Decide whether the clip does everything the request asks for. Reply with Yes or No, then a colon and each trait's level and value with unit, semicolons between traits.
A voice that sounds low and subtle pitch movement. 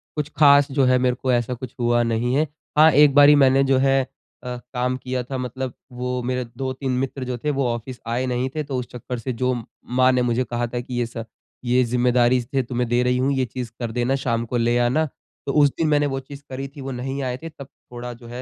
Yes: low, 125 Hz; narrow, 1.7 semitones